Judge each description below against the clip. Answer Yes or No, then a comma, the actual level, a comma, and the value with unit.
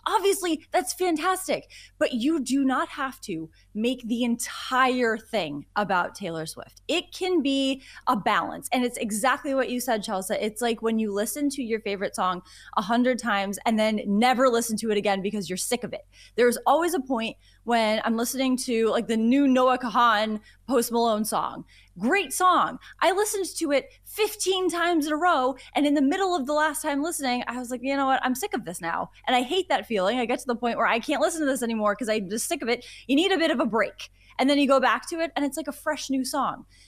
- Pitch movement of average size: Yes, average, 4.9 semitones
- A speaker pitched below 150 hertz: No, very high, 255 Hz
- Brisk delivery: Yes, fast, 230 wpm